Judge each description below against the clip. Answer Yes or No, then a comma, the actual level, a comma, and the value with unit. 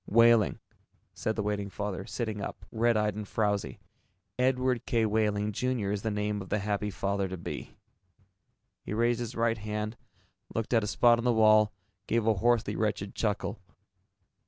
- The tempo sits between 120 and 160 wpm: No, average, 170 wpm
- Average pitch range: No, narrow, 2.1 semitones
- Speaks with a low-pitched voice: Yes, low, 105 Hz